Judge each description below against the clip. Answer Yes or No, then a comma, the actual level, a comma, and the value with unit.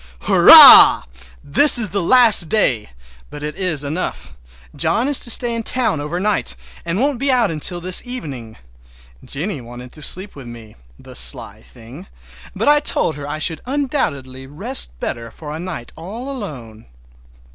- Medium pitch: Yes, medium, 160 Hz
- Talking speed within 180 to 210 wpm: No, average, 160 wpm